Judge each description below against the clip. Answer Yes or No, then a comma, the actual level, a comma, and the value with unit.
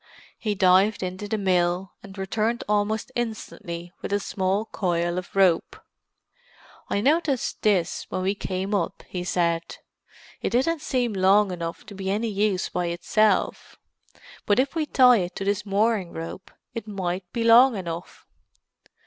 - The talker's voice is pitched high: Yes, high, 195 Hz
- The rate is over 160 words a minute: No, average, 155 wpm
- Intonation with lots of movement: No, average, 3.3 semitones